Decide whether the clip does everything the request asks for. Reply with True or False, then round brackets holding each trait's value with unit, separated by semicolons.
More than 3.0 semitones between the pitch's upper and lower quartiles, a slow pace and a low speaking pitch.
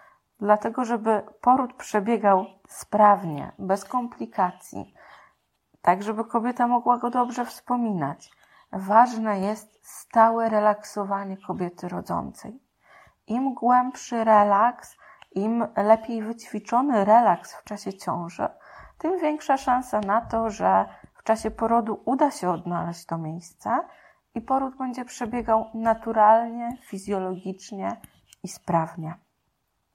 False (3.7 semitones; 105 wpm; 225 Hz)